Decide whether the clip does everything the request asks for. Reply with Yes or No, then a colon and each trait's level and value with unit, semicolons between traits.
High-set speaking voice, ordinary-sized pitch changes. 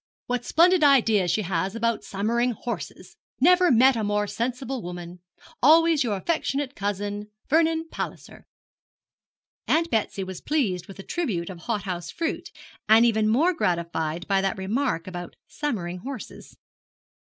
No: high, 220 Hz; wide, 6.5 semitones